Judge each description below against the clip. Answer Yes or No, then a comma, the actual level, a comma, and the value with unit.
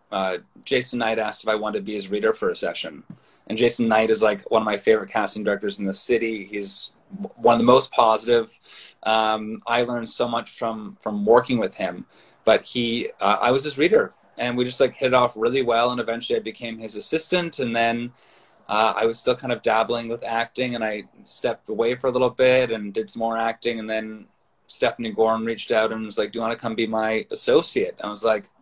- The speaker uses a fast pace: Yes, fast, 235 wpm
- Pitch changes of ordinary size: No, narrow, 1.8 semitones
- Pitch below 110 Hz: No, low, 115 Hz